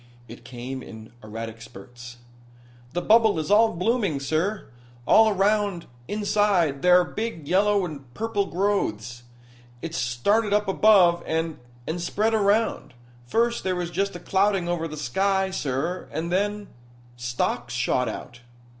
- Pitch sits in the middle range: Yes, medium, 175 Hz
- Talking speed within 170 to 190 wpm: No, average, 145 wpm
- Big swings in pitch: Yes, wide, 7.4 semitones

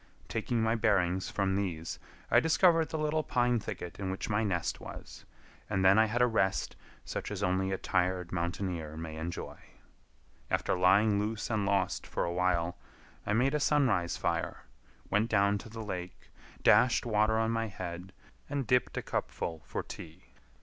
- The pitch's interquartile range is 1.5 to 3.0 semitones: No, average, 3.7 semitones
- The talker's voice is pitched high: No, low, 100 Hz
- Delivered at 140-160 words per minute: No, average, 170 wpm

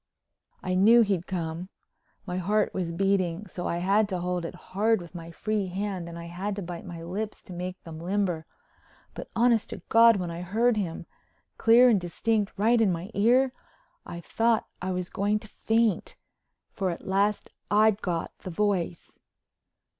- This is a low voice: No, high, 190 Hz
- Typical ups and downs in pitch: Yes, average, 3.5 semitones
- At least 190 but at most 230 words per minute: No, average, 170 wpm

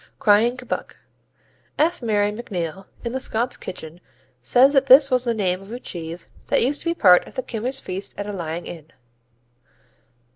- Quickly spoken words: No, average, 180 wpm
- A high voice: Yes, high, 215 Hz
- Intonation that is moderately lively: No, wide, 5.8 semitones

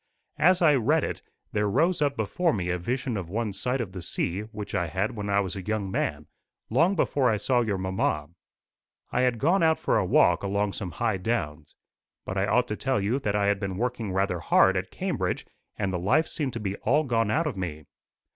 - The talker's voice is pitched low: Yes, low, 105 Hz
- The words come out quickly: Yes, fast, 225 wpm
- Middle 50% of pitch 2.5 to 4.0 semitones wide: No, average, 5.0 semitones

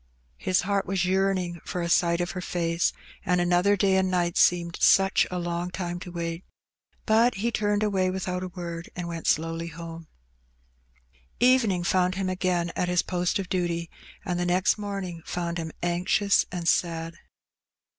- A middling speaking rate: Yes, average, 170 wpm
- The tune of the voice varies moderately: No, narrow, 1.8 semitones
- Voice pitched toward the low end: No, medium, 180 Hz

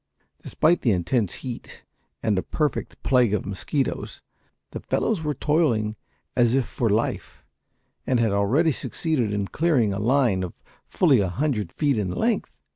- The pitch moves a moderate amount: No, wide, 6.0 semitones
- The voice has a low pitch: Yes, low, 120 Hz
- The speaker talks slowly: No, average, 155 wpm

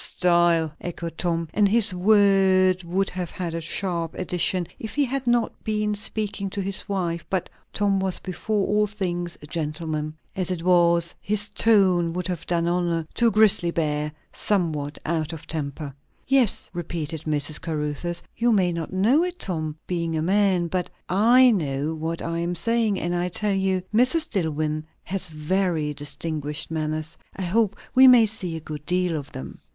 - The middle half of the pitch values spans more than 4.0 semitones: No, average, 3.7 semitones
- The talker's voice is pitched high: No, medium, 175 Hz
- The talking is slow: No, average, 175 wpm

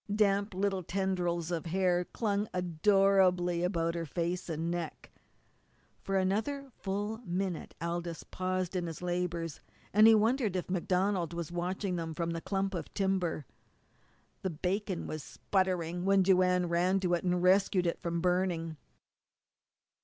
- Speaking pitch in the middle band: Yes, medium, 180 Hz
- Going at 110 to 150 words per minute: Yes, average, 145 wpm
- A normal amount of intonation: No, narrow, 2.2 semitones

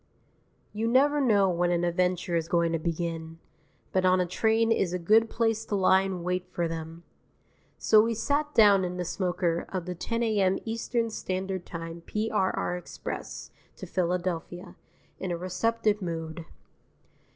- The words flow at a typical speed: Yes, average, 160 wpm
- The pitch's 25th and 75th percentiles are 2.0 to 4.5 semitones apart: Yes, average, 4.0 semitones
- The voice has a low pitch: No, medium, 185 Hz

